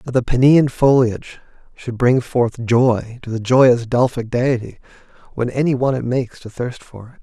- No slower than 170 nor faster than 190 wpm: Yes, average, 185 wpm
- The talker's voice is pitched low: Yes, low, 125 Hz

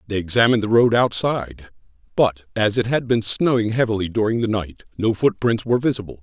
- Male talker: Yes, male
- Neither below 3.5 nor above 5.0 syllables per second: No, 5.9 syllables/s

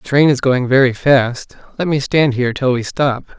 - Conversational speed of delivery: No, fast, 230 wpm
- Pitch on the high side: No, low, 130 Hz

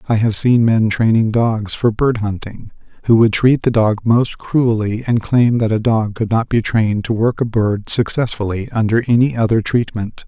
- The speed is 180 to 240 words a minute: Yes, average, 200 wpm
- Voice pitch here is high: No, low, 110 Hz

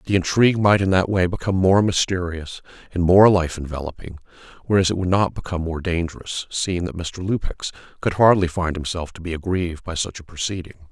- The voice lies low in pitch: Yes, very low, 90 Hz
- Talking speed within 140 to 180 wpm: No, average, 190 wpm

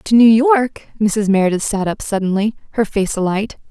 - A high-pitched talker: Yes, high, 210 Hz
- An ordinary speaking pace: Yes, average, 180 wpm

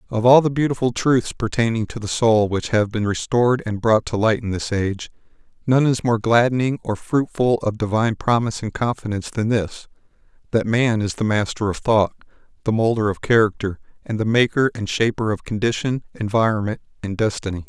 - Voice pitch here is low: Yes, low, 115 Hz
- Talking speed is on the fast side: No, average, 180 wpm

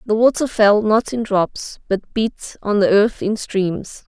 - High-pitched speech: Yes, high, 210 Hz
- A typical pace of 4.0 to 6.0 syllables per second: No, 3.7 syllables/s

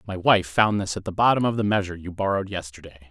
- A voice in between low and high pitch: No, very low, 95 Hz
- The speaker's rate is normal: No, fast, 250 wpm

